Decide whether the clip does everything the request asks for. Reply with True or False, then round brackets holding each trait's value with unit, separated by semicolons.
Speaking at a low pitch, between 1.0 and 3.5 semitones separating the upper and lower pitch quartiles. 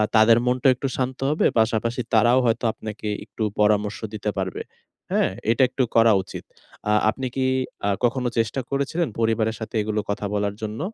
True (115 Hz; 2.8 semitones)